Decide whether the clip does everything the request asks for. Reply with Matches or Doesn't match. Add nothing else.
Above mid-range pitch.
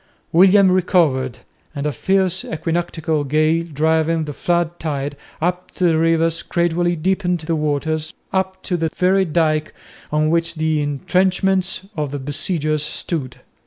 Doesn't match